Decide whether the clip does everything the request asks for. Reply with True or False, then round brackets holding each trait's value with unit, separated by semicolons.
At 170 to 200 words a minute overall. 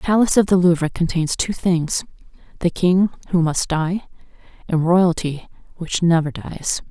False (150 wpm)